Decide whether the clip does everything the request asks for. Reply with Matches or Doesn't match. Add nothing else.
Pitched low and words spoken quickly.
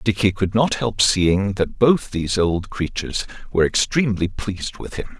Doesn't match